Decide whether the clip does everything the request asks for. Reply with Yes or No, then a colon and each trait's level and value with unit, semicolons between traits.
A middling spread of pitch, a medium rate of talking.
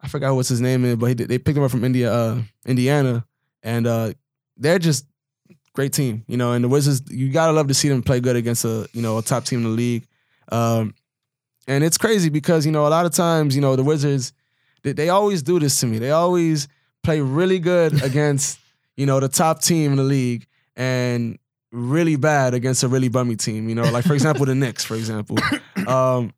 No: average, 3.5 semitones; fast, 225 wpm